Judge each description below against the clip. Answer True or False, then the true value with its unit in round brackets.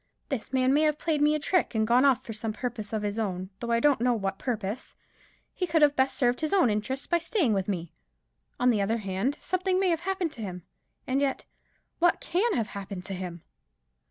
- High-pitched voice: True (245 Hz)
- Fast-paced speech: True (225 wpm)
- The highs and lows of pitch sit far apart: True (6.4 semitones)